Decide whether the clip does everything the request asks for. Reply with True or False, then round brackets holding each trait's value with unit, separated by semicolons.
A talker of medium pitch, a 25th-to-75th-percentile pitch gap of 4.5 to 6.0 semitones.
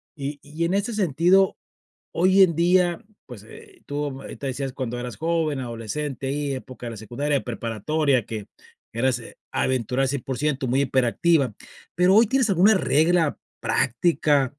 True (145 Hz; 4.9 semitones)